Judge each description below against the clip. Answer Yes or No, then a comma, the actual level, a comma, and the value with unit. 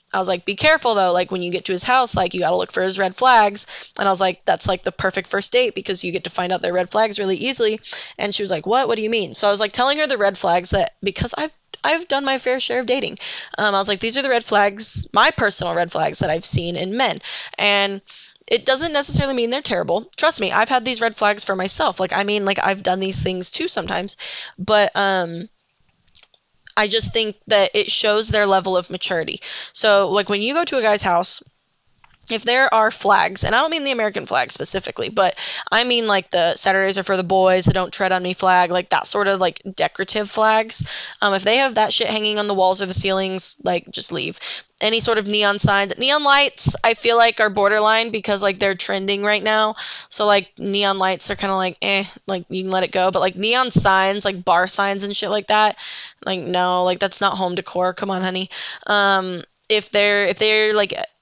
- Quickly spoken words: Yes, fast, 240 wpm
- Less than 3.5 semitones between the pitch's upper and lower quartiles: Yes, average, 2.9 semitones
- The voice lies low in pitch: No, high, 200 Hz